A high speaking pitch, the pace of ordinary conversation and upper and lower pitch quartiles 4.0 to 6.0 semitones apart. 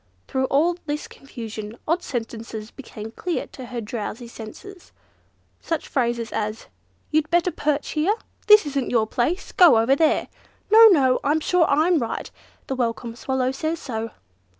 Yes: very high, 265 Hz; average, 150 wpm; wide, 5.6 semitones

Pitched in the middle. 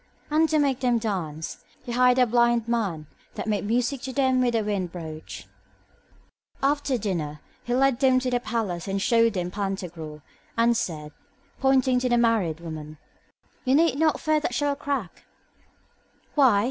No: high, 235 Hz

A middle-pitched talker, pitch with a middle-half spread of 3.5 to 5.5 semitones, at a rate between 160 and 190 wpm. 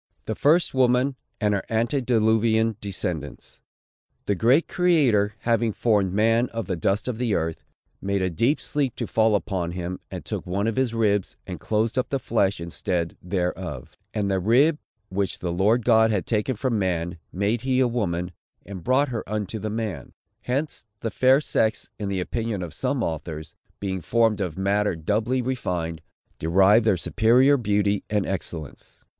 No: low, 105 Hz; average, 4.0 semitones; average, 170 wpm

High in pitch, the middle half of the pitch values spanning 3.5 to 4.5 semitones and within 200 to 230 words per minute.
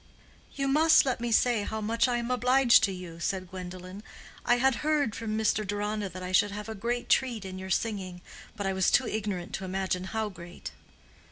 Yes: high, 210 Hz; average, 4.2 semitones; fast, 205 wpm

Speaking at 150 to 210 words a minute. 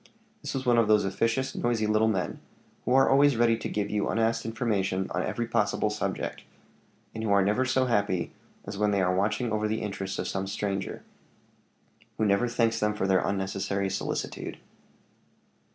Yes: average, 180 wpm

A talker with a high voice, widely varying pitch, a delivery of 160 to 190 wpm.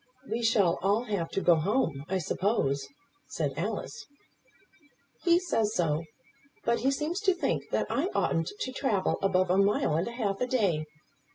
Yes: high, 200 Hz; wide, 6.0 semitones; average, 170 wpm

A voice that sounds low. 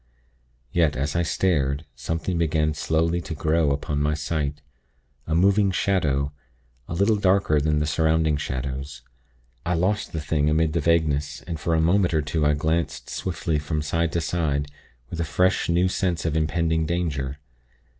Yes: very low, 80 Hz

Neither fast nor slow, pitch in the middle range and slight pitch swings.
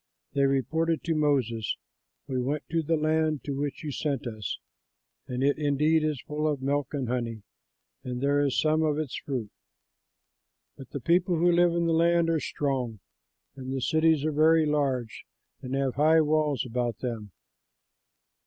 No: average, 170 wpm; medium, 145 Hz; average, 3.4 semitones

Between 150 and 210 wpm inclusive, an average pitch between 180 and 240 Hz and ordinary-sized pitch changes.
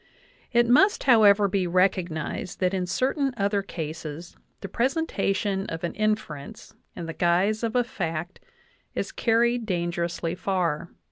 No: average, 140 wpm; high, 190 Hz; average, 4.7 semitones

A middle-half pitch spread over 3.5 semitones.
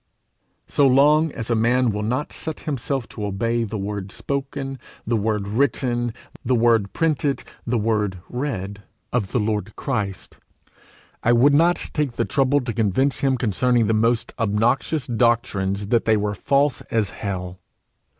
Yes: average, 4.4 semitones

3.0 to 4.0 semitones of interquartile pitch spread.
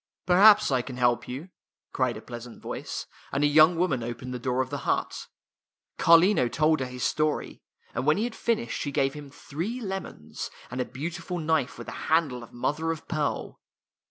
No: average, 4.9 semitones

